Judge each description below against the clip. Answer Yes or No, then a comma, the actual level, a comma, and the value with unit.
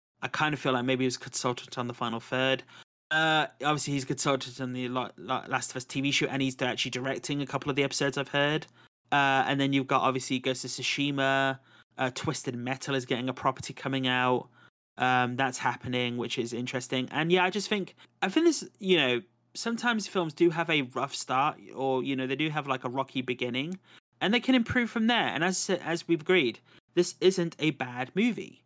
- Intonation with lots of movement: No, average, 3.6 semitones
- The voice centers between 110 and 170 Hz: Yes, low, 135 Hz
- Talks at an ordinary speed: No, fast, 215 wpm